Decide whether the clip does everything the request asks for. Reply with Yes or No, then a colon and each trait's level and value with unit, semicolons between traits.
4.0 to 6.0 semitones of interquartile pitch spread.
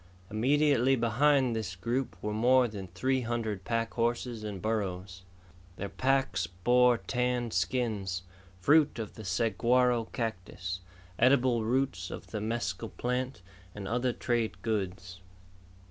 Yes: average, 4.3 semitones